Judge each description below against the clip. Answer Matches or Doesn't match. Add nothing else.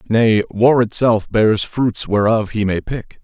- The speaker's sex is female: Doesn't match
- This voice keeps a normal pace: Matches